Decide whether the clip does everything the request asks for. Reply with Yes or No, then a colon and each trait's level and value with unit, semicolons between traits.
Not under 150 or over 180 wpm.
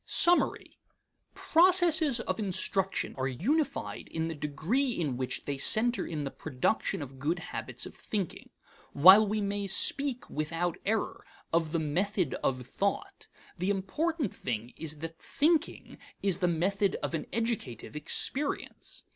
No: average, 140 wpm